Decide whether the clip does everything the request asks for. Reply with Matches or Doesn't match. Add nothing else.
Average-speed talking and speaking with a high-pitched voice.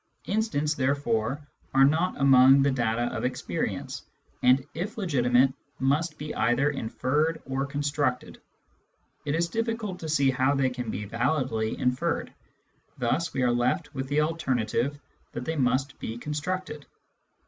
Doesn't match